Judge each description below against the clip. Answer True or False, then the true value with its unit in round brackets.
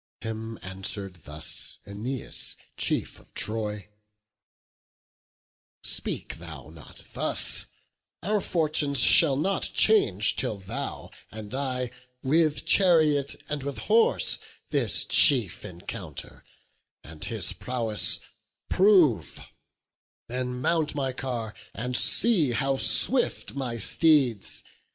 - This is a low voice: True (125 Hz)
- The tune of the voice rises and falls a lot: True (5.8 semitones)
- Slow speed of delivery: True (100 wpm)